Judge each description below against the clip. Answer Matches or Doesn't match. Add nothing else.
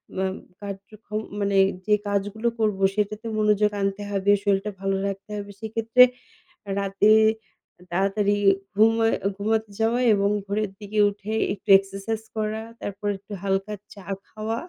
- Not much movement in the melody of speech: Matches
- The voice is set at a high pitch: Matches